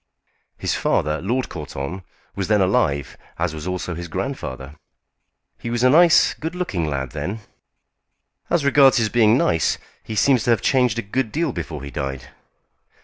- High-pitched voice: No, low, 100 Hz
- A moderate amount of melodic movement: No, wide, 8.7 semitones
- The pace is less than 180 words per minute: Yes, average, 165 wpm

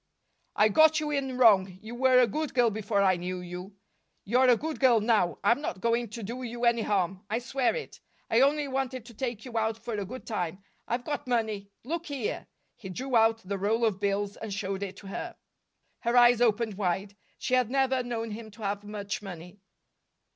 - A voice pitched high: Yes, high, 225 Hz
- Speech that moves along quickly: Yes, fast, 210 wpm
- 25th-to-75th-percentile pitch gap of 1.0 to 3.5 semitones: No, average, 3.9 semitones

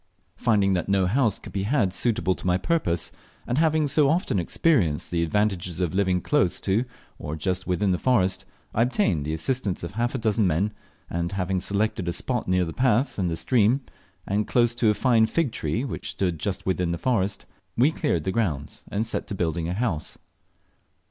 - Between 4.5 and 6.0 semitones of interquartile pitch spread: Yes, average, 5.0 semitones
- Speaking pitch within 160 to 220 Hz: No, low, 100 Hz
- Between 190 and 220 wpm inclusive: Yes, average, 200 wpm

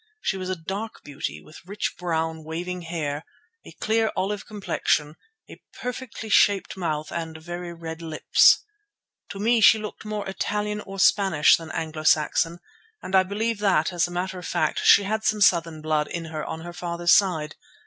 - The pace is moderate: Yes, average, 180 wpm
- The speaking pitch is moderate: Yes, medium, 175 Hz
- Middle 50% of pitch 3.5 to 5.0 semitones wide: Yes, average, 4.0 semitones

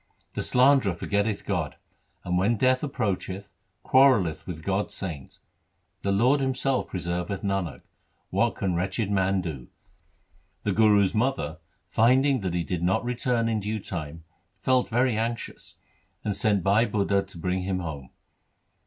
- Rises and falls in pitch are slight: No, average, 4.6 semitones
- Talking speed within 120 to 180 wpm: Yes, average, 150 wpm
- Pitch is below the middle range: Yes, low, 100 Hz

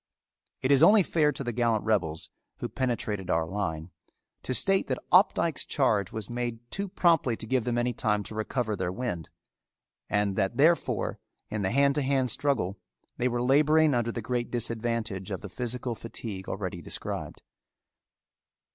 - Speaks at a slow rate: No, average, 165 wpm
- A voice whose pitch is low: Yes, low, 120 Hz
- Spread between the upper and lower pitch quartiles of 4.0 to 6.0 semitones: Yes, average, 4.6 semitones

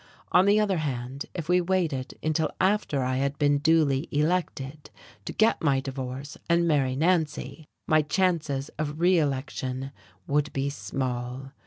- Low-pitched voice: No, medium, 145 Hz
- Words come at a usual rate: Yes, average, 145 wpm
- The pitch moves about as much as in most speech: Yes, average, 3.7 semitones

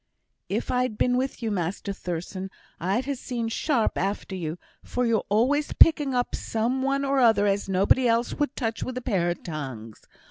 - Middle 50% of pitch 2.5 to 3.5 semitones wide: No, average, 4.9 semitones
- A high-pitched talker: Yes, high, 225 Hz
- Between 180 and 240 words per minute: Yes, average, 185 wpm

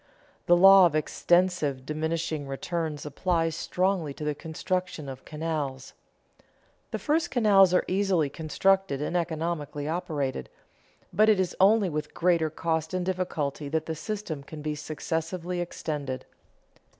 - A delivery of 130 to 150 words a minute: Yes, slow, 135 wpm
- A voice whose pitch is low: No, medium, 165 Hz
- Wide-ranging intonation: No, average, 3.4 semitones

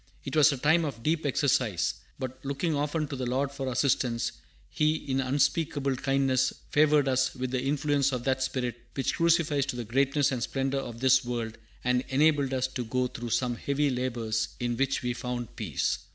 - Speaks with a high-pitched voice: No, low, 135 Hz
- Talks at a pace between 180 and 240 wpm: Yes, average, 190 wpm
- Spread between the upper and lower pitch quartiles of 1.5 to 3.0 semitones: Yes, narrow, 2.4 semitones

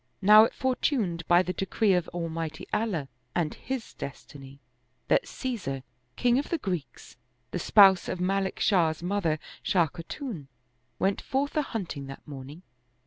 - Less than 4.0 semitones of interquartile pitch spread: No, average, 5.3 semitones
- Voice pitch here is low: No, medium, 180 Hz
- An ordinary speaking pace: Yes, average, 150 wpm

